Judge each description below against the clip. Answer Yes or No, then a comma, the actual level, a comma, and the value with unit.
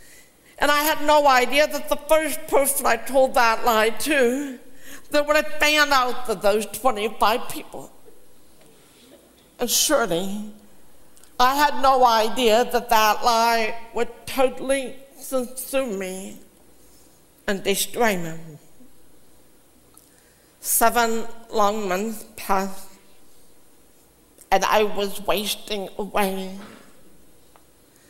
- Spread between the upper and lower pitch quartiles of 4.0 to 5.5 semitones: Yes, average, 4.3 semitones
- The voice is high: Yes, high, 235 Hz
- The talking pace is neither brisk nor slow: No, slow, 105 wpm